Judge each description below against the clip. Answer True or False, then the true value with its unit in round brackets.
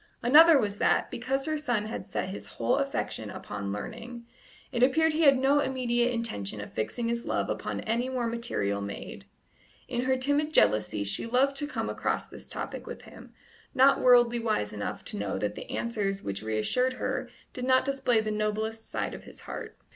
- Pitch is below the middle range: False (235 Hz)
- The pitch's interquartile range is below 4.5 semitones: False (5.1 semitones)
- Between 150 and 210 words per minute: True (190 wpm)